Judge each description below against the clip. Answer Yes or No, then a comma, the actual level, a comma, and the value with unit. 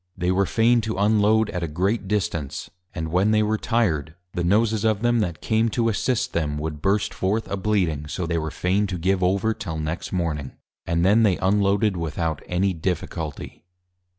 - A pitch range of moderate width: Yes, average, 4.3 semitones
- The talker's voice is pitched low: Yes, very low, 95 Hz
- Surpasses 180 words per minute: Yes, average, 190 wpm